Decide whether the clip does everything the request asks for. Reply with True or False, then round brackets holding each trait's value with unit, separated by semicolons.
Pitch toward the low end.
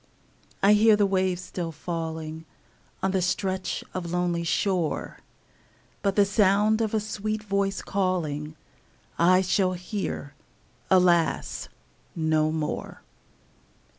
False (185 Hz)